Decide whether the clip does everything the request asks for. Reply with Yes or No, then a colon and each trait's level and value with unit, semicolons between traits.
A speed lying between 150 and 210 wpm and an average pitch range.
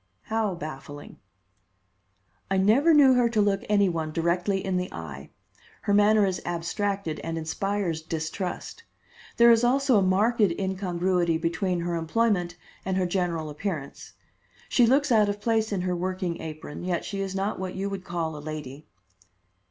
Yes: average, 160 wpm; average, 3.5 semitones